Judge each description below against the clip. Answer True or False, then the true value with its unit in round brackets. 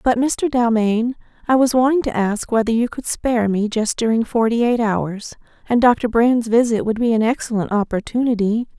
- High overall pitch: True (230 Hz)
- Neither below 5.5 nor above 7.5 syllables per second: False (5.0 syllables/s)